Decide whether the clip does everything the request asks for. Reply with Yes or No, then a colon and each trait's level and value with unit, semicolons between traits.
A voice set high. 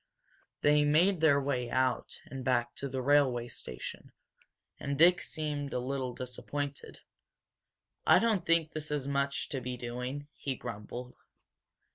No: medium, 140 Hz